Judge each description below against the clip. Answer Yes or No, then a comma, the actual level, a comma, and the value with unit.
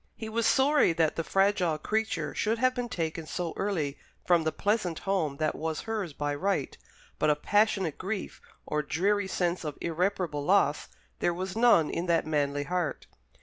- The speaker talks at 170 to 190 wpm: Yes, average, 175 wpm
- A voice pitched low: No, medium, 175 Hz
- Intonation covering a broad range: No, average, 4.7 semitones